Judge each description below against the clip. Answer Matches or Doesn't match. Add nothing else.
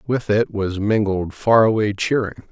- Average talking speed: Matches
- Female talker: Doesn't match